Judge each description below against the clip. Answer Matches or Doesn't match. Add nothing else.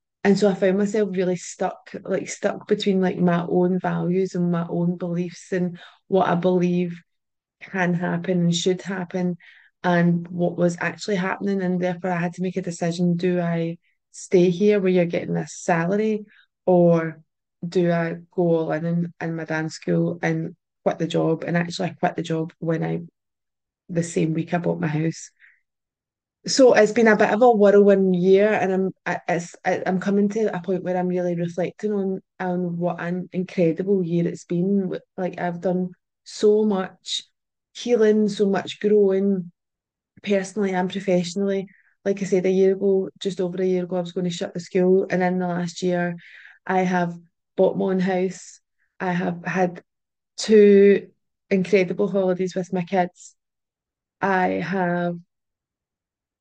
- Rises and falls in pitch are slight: Matches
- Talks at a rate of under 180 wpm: Matches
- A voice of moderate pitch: Matches